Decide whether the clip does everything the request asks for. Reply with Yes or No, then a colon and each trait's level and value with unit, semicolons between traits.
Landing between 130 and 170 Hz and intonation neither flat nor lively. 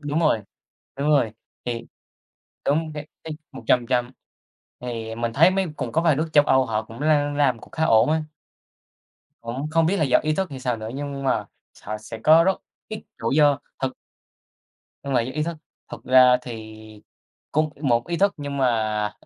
Yes: low, 135 Hz; average, 4.8 semitones